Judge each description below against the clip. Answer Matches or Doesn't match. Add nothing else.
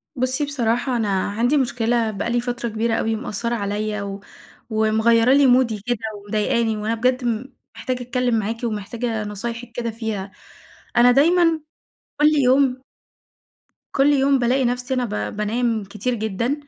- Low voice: Doesn't match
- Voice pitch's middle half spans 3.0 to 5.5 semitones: Doesn't match